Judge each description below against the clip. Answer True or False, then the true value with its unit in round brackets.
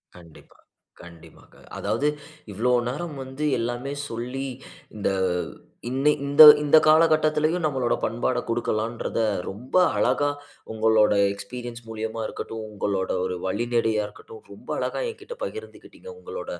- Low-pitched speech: True (120 Hz)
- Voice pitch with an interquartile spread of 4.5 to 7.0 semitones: True (5.2 semitones)